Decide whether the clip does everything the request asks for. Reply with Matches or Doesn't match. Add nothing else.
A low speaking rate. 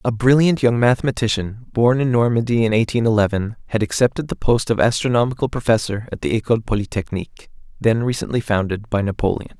Doesn't match